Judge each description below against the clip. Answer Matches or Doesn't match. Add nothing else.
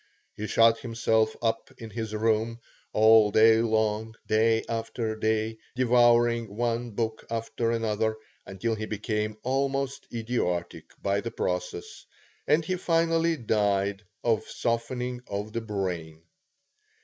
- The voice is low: Matches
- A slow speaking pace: Matches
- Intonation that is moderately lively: Doesn't match